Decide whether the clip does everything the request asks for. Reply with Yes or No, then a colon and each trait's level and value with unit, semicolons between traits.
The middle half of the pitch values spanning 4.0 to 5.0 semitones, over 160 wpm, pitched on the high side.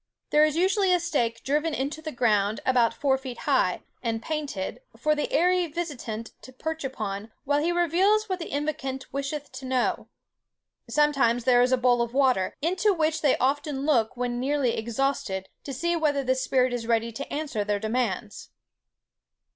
Yes: average, 4.5 semitones; average, 175 wpm; very high, 270 Hz